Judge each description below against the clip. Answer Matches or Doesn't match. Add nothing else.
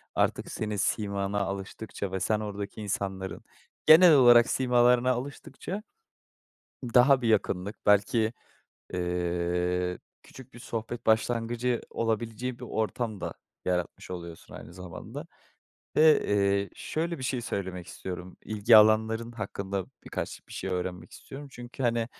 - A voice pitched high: Doesn't match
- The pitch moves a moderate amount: Matches